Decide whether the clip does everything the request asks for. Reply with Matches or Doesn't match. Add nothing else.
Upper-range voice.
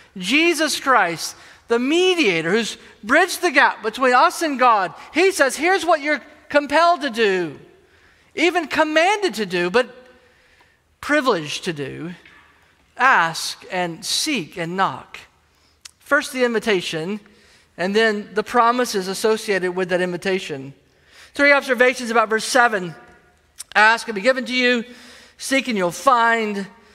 Matches